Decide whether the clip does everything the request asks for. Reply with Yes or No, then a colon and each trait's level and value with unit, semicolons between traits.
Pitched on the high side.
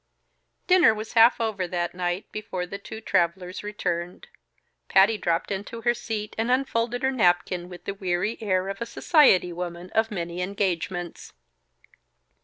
Yes: high, 195 Hz